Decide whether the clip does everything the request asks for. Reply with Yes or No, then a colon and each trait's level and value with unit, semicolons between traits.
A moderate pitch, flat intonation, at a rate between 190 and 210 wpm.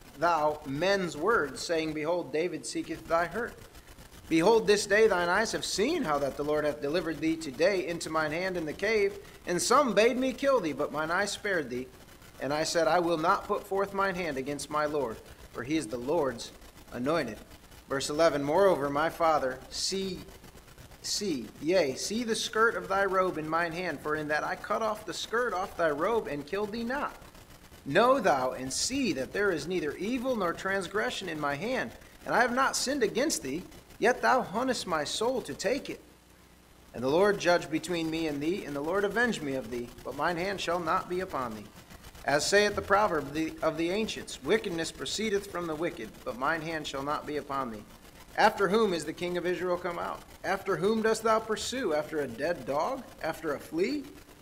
No: medium, 175 Hz; average, 5.1 semitones; fast, 205 wpm